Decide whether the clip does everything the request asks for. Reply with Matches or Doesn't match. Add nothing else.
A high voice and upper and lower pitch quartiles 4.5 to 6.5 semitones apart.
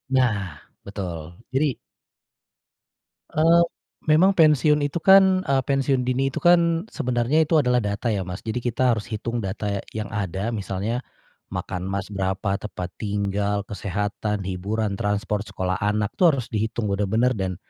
Doesn't match